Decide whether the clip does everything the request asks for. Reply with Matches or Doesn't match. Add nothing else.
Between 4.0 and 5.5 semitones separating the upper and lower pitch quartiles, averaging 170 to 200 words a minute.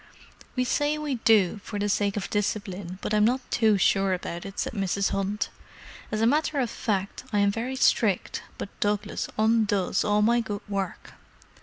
Doesn't match